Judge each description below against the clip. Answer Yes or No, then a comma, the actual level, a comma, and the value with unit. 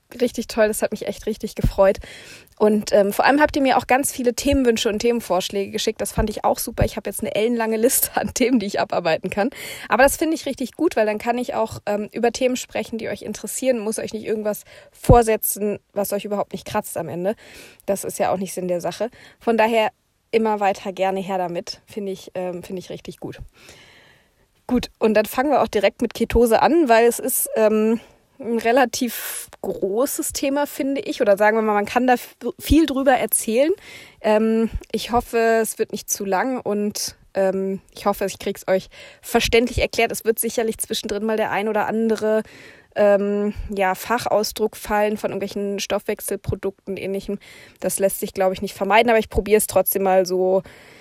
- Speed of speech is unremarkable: No, fast, 200 wpm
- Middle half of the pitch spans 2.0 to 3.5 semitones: Yes, average, 2.9 semitones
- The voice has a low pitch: No, high, 215 Hz